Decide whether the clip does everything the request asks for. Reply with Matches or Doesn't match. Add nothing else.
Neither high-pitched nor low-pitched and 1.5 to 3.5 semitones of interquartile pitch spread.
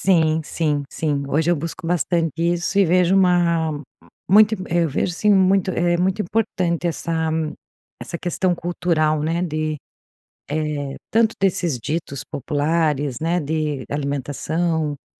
Matches